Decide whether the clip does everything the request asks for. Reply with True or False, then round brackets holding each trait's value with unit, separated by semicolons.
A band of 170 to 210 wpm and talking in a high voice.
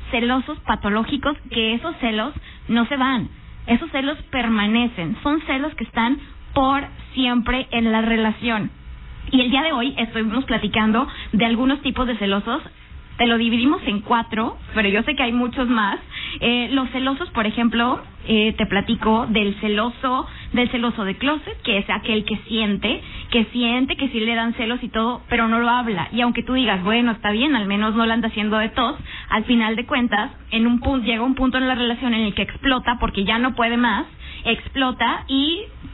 True (190 wpm; 235 Hz)